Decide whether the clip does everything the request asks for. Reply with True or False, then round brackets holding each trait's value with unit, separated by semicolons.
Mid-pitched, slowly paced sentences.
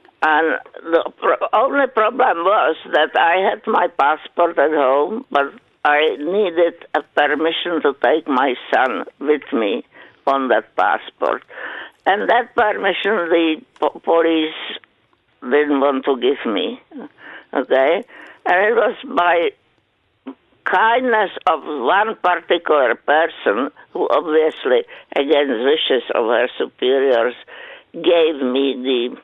True (170 Hz; 115 wpm)